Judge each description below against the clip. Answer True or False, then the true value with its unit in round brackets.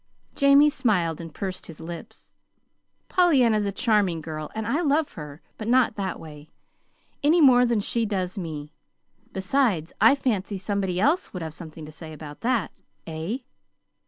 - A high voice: True (195 Hz)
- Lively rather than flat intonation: True (7.0 semitones)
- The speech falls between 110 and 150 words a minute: False (160 wpm)